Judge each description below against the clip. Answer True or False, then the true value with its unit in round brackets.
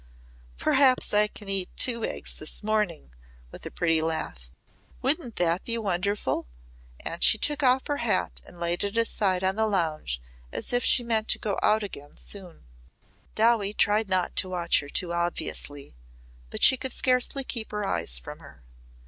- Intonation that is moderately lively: True (5.0 semitones)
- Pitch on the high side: True (200 Hz)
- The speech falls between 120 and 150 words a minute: False (175 wpm)